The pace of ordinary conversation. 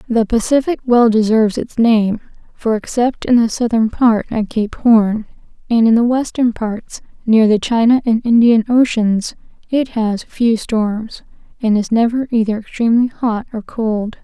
Yes: average, 160 wpm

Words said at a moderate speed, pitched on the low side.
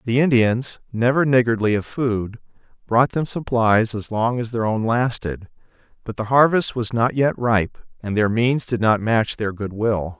Yes: average, 185 wpm; low, 115 Hz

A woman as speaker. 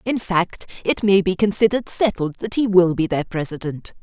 Yes: female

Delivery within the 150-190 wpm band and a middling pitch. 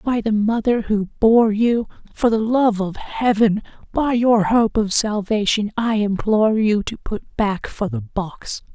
No: average, 160 wpm; high, 215 Hz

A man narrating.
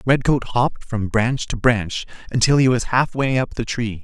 Yes: male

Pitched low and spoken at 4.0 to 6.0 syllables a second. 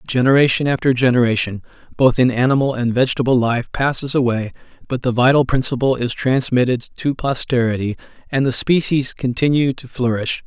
Yes: low, 125 Hz; 5.6 syllables/s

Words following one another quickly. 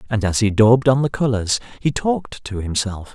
Yes: fast, 210 wpm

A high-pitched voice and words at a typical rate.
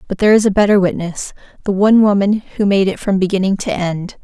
No: high, 195 Hz; fast, 225 wpm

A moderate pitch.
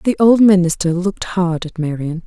Yes: medium, 180 Hz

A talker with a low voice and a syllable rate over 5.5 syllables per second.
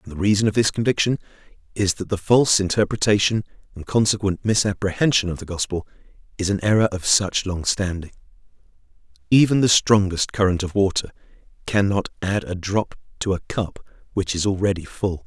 Yes: low, 100 Hz; 5.7 syllables/s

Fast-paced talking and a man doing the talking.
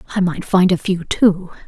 No: fast, 215 wpm; female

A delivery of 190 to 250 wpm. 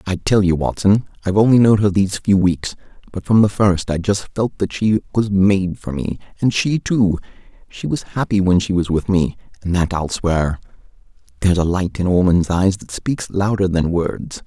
Yes: fast, 205 wpm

